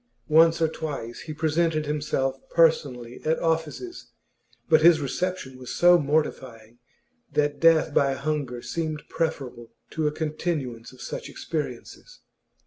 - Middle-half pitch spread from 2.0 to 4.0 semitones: Yes, average, 3.4 semitones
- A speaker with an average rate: No, slow, 130 wpm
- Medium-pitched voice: Yes, medium, 150 Hz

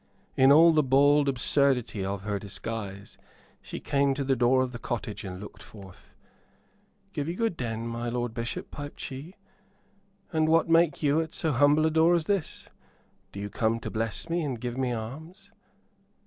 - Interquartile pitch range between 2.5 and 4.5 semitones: No, wide, 5.5 semitones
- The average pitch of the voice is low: Yes, low, 130 Hz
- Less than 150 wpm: No, average, 180 wpm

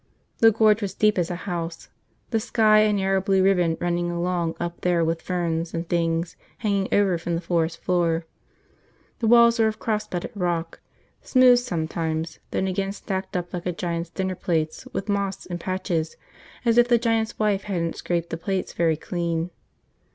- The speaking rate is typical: Yes, average, 180 wpm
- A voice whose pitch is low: No, medium, 180 Hz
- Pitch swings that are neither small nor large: Yes, average, 3.3 semitones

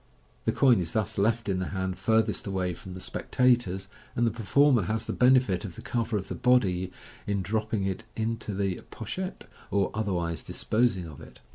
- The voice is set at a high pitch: No, low, 105 Hz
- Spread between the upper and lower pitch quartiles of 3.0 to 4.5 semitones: Yes, average, 3.7 semitones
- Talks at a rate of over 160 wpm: Yes, average, 185 wpm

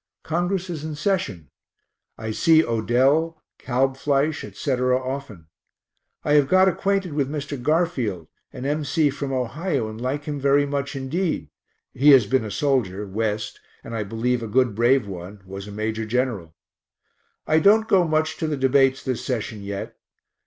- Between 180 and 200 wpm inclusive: No, average, 160 wpm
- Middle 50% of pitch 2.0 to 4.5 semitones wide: No, average, 5.3 semitones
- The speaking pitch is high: No, low, 135 Hz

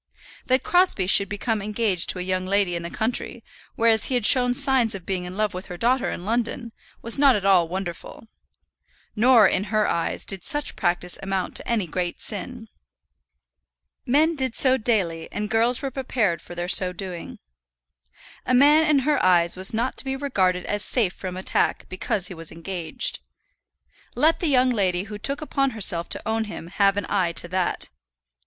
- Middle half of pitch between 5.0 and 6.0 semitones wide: Yes, average, 5.3 semitones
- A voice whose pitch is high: Yes, high, 205 Hz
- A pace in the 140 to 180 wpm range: No, average, 190 wpm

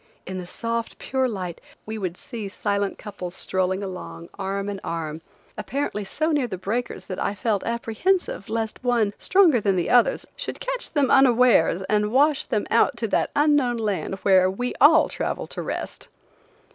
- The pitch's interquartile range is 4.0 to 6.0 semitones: Yes, average, 4.7 semitones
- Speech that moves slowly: No, average, 170 wpm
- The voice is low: No, high, 215 Hz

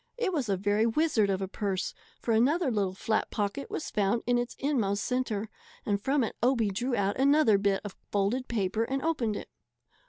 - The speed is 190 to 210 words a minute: Yes, average, 195 wpm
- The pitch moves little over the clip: No, average, 4.7 semitones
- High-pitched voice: Yes, high, 225 Hz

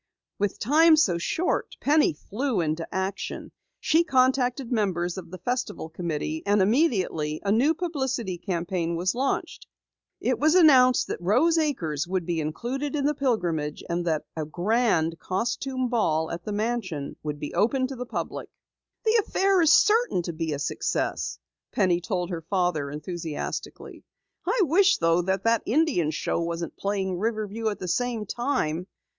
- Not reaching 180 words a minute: Yes, average, 160 wpm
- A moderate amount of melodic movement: No, wide, 7.5 semitones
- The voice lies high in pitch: Yes, high, 200 Hz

